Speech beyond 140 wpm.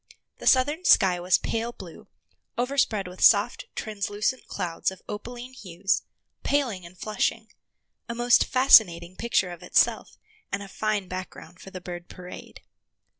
No: slow, 135 wpm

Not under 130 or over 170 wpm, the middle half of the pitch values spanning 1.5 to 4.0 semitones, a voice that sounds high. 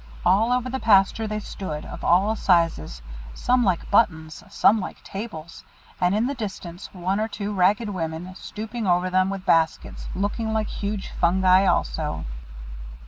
Yes: average, 155 wpm; average, 3.3 semitones; high, 195 Hz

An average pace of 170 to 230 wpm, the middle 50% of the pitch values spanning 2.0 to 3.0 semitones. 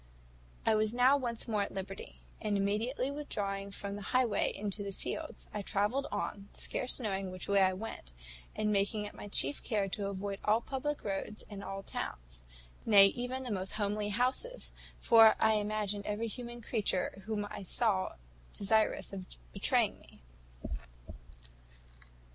No: average, 155 wpm; average, 2.7 semitones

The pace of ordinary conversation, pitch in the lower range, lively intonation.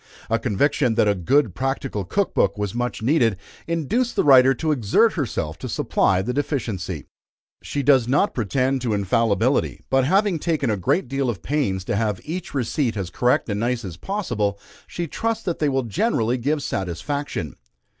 Yes: average, 175 wpm; low, 125 Hz; wide, 5.9 semitones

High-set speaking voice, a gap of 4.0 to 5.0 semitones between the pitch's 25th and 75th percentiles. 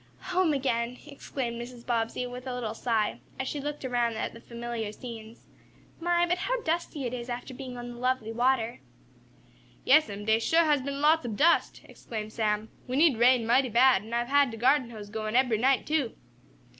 No: high, 245 Hz; average, 3.3 semitones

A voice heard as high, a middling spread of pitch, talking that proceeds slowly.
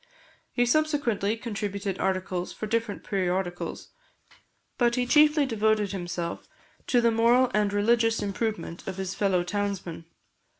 Yes: high, 210 Hz; average, 3.6 semitones; slow, 125 wpm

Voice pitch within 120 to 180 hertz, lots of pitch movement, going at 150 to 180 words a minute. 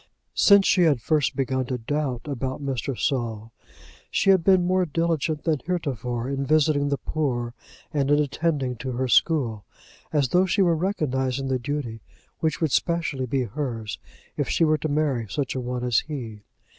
No: medium, 140 Hz; average, 3.9 semitones; average, 175 wpm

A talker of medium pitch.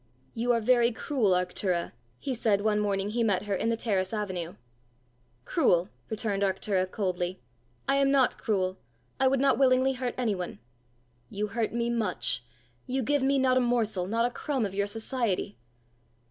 No: high, 220 Hz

